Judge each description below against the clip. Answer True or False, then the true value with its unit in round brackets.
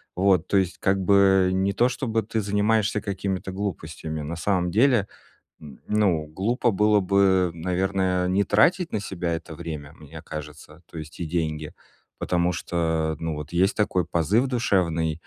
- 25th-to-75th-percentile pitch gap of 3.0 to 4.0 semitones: True (3.7 semitones)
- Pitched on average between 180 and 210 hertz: False (90 Hz)